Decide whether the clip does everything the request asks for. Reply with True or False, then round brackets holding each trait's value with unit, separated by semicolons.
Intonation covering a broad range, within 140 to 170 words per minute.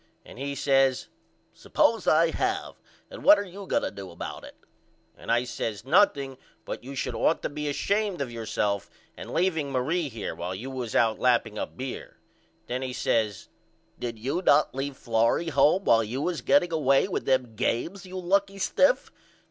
False (7.1 semitones; 180 wpm)